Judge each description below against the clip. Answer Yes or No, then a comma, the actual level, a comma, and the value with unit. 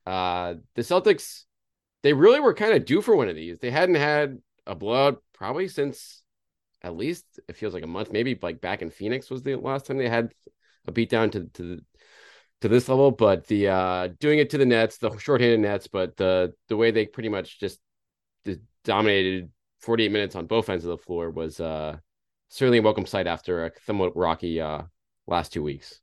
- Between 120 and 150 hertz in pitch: No, low, 105 Hz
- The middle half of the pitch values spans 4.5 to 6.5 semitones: Yes, wide, 5.4 semitones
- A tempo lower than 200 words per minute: No, fast, 205 wpm